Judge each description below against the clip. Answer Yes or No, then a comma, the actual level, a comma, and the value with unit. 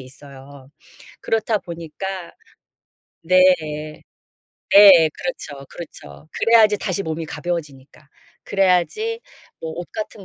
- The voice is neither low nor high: Yes, medium, 175 Hz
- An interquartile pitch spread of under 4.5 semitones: No, average, 5.2 semitones